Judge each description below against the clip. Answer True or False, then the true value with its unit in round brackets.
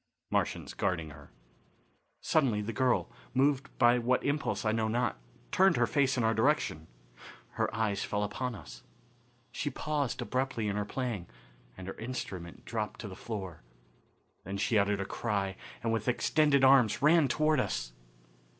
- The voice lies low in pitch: True (115 Hz)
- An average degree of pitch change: True (4.7 semitones)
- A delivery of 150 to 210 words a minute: True (160 wpm)